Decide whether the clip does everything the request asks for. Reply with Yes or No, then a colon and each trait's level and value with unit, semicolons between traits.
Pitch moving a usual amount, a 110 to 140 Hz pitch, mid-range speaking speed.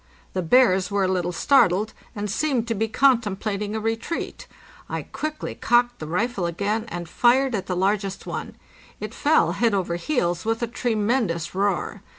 No: average, 4.3 semitones; high, 210 Hz; average, 165 wpm